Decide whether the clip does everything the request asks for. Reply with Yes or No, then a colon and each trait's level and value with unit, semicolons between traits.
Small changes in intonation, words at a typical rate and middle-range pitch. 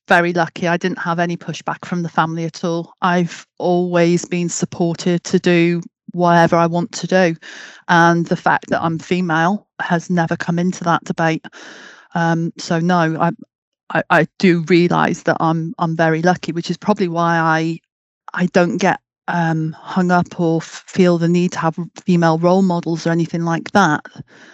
Yes: narrow, 1.3 semitones; average, 180 wpm; medium, 170 Hz